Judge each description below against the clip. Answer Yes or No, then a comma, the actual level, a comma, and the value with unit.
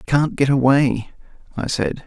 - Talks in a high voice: No, low, 135 Hz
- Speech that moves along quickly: No, average, 145 wpm